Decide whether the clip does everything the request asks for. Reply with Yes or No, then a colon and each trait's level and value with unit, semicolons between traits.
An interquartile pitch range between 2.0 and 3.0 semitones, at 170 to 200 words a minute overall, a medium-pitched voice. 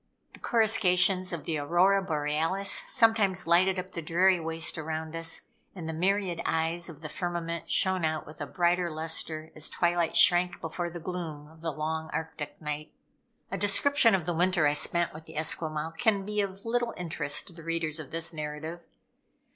Yes: average, 2.7 semitones; average, 180 wpm; medium, 170 Hz